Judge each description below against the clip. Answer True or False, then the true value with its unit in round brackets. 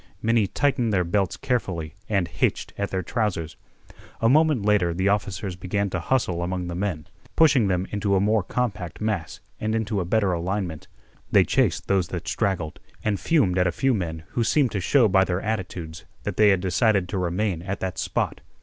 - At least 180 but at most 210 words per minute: True (195 wpm)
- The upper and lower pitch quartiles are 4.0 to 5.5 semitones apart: False (3.5 semitones)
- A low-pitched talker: True (100 Hz)